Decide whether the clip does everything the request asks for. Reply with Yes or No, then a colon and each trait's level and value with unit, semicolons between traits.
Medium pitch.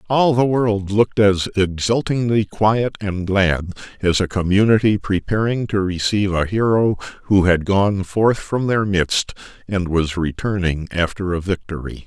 No: low, 100 Hz